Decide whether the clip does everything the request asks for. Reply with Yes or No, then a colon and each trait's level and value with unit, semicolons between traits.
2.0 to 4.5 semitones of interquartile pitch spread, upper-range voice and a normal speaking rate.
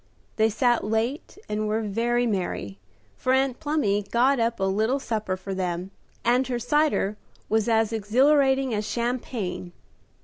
Yes: average, 3.7 semitones; high, 225 Hz; average, 145 wpm